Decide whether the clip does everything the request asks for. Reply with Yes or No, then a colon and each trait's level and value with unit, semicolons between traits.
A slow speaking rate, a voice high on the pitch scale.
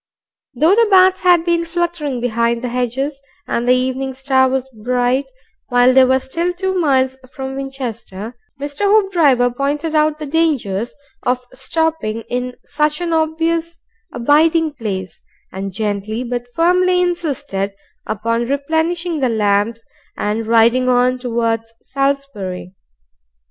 Yes: slow, 130 wpm; very high, 265 Hz